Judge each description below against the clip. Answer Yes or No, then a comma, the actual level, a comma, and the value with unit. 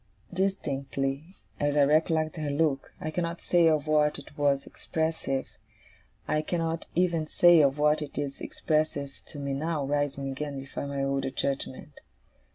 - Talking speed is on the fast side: No, average, 155 wpm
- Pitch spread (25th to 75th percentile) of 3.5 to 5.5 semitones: No, narrow, 2.4 semitones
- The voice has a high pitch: No, medium, 150 Hz